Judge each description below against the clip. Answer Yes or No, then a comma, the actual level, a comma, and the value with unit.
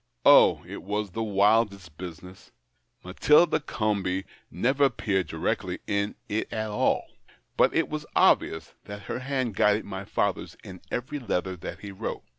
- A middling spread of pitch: Yes, average, 4.0 semitones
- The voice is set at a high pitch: No, low, 105 Hz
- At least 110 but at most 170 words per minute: Yes, average, 150 wpm